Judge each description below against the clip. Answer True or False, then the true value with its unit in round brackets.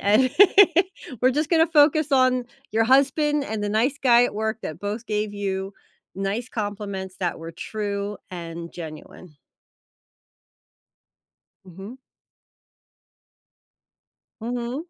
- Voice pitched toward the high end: True (215 Hz)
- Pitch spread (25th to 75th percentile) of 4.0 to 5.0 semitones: True (4.7 semitones)